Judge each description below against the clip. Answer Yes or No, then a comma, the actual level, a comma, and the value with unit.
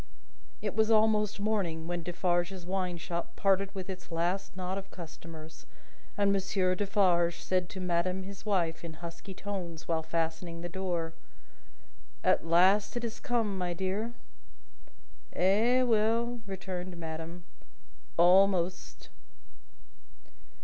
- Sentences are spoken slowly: Yes, slow, 120 wpm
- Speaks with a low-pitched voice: No, medium, 185 Hz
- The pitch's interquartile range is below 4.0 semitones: Yes, average, 2.7 semitones